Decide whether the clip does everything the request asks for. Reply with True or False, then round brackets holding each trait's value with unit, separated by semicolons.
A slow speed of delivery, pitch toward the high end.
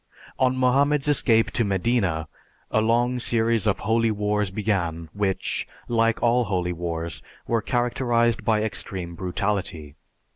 False (130 wpm; 110 Hz)